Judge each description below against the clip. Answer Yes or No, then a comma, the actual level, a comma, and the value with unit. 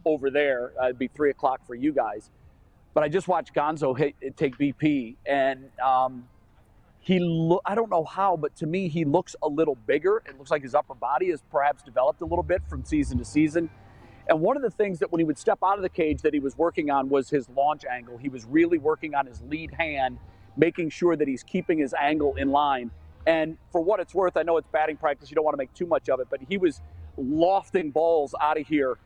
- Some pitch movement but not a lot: Yes, average, 4.2 semitones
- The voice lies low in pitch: No, medium, 155 Hz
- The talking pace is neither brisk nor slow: No, fast, 235 wpm